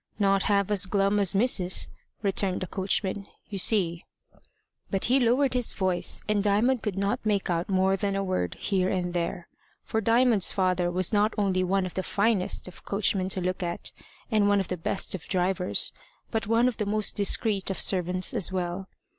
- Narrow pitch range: Yes, narrow, 2.2 semitones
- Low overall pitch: No, high, 195 Hz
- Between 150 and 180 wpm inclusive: No, average, 195 wpm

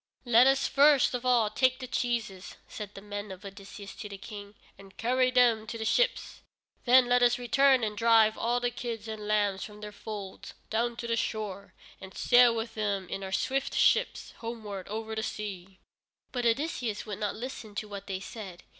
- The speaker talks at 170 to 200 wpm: Yes, average, 195 wpm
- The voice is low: No, high, 220 Hz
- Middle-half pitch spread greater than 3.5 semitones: No, average, 3.1 semitones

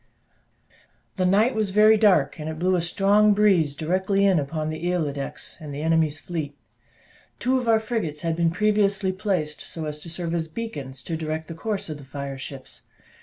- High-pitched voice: No, medium, 170 Hz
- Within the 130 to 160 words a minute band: No, average, 195 wpm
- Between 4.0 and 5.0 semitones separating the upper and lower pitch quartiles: Yes, average, 4.6 semitones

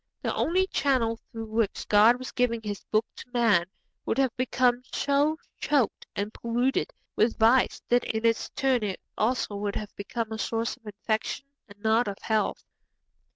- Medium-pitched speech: No, high, 230 Hz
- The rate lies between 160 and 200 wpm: Yes, average, 170 wpm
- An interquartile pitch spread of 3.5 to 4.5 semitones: No, average, 2.7 semitones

